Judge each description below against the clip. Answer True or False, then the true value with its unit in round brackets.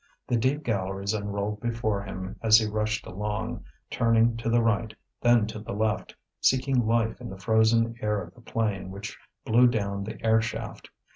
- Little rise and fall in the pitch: True (2.0 semitones)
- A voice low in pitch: True (110 Hz)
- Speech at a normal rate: True (175 wpm)